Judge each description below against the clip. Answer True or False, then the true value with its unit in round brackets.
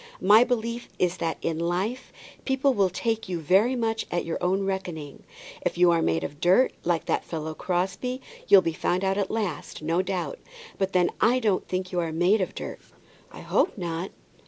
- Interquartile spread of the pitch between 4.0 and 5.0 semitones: True (4.3 semitones)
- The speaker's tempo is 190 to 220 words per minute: True (195 wpm)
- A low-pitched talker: False (185 Hz)